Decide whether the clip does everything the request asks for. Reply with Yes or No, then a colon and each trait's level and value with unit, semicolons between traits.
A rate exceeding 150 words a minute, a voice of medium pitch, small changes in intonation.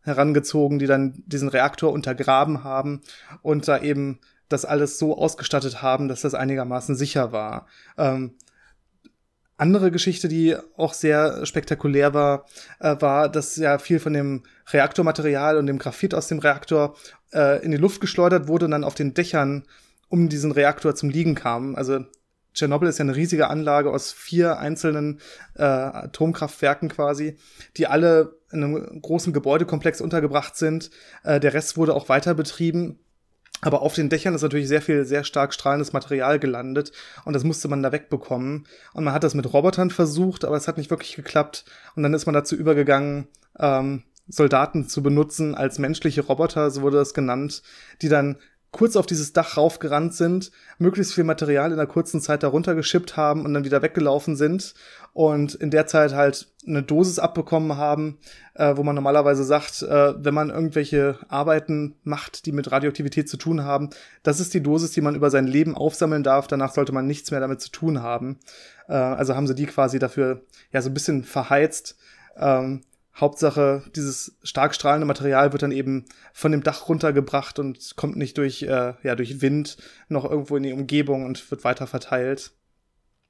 Yes: average, 180 wpm; medium, 145 Hz; narrow, 2.1 semitones